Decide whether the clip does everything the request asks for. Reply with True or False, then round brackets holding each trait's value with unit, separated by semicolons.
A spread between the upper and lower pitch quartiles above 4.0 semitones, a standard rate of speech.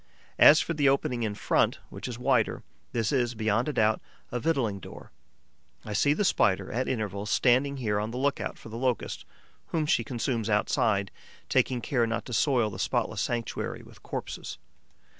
False (3.5 semitones; 180 wpm)